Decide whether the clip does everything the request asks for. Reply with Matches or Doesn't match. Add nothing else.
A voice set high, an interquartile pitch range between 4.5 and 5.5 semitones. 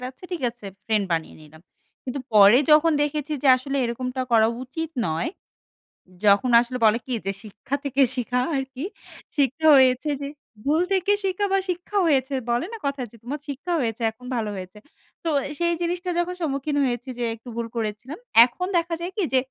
Matches